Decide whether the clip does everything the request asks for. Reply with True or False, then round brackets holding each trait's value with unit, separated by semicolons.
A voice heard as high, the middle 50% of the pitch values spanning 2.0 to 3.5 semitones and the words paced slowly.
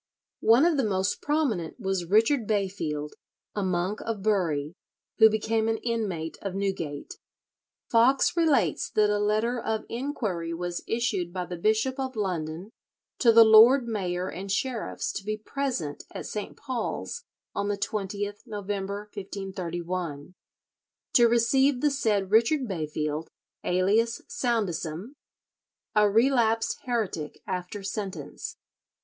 False (205 Hz; 4.1 semitones; 130 wpm)